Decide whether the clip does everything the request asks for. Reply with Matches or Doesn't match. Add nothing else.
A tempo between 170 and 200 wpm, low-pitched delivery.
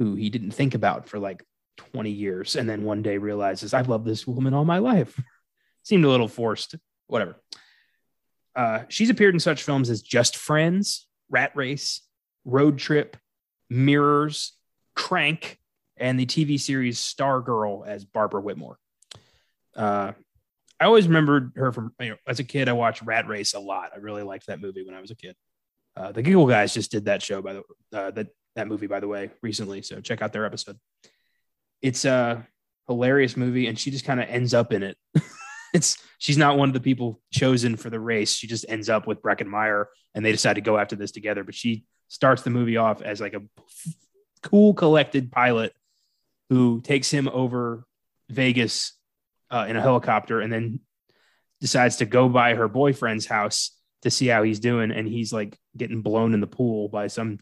Matches